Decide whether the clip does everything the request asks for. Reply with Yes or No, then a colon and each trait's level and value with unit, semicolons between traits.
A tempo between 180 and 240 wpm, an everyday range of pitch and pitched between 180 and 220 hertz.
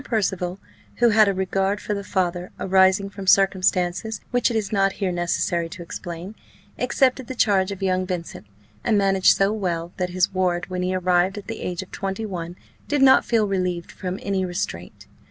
No: average, 190 wpm; narrow, 2.0 semitones; high, 190 Hz